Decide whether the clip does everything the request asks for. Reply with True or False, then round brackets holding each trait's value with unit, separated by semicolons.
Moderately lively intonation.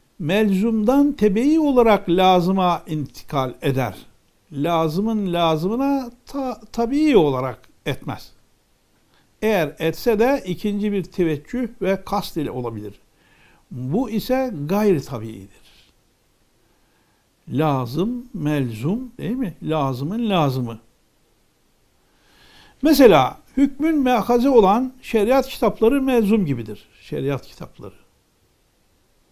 False (8.3 semitones)